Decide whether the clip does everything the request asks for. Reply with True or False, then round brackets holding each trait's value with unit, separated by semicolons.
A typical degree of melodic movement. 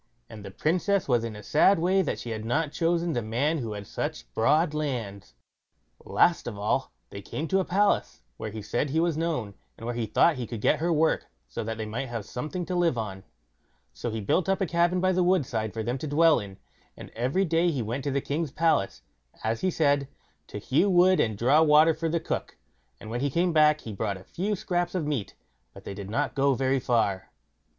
False (7.0 semitones)